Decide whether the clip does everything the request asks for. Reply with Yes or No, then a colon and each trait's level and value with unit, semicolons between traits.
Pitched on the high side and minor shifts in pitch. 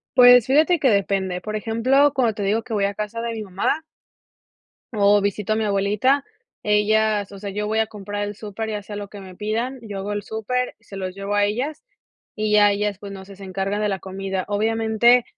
Yes: high, 210 Hz; narrow, 2.1 semitones